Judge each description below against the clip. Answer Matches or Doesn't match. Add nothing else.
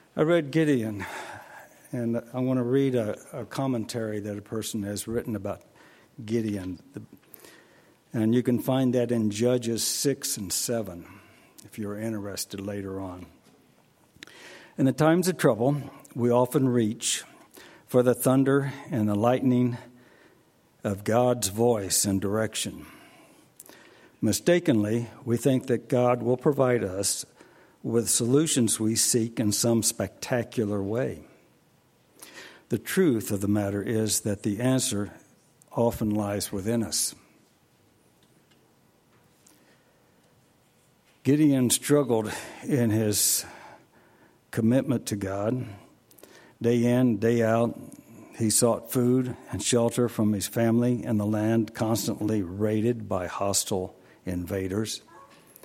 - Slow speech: Matches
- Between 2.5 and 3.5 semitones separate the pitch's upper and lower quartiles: Matches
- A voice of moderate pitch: Doesn't match